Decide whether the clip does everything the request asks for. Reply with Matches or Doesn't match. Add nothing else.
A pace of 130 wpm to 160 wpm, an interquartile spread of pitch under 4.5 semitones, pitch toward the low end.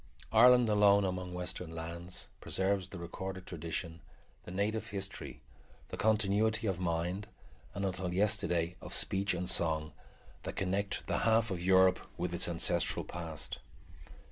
Matches